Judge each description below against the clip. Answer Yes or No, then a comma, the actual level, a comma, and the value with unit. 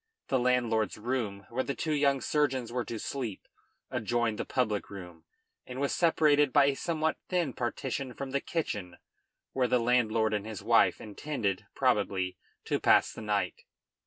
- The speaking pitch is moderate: No, low, 125 Hz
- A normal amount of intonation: Yes, average, 4.4 semitones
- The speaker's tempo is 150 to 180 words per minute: Yes, average, 160 wpm